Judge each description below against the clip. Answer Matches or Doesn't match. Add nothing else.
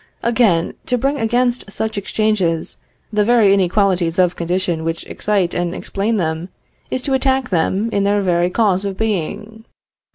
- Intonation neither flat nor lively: Matches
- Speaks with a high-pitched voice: Matches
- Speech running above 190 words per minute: Doesn't match